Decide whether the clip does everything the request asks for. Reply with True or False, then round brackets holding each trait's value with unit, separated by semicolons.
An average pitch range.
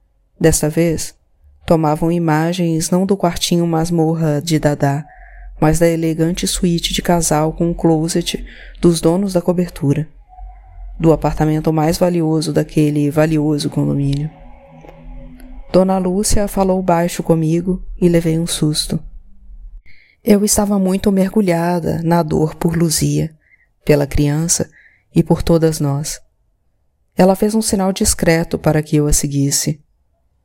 True (3.0 semitones)